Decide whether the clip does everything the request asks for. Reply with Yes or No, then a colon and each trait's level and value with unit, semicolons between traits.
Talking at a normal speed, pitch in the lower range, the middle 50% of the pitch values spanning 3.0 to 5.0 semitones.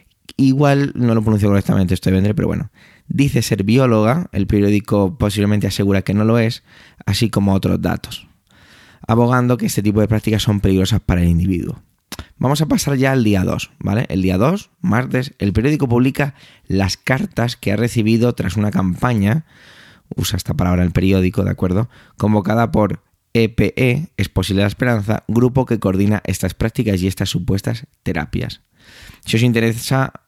Yes: average, 165 wpm; low, 110 Hz; average, 3.8 semitones